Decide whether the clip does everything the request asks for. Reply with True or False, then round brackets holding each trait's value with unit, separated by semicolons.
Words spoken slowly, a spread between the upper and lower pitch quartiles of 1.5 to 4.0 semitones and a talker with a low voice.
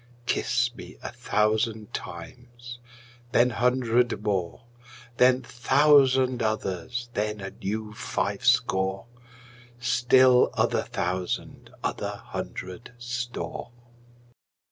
True (90 wpm; 2.8 semitones; 120 Hz)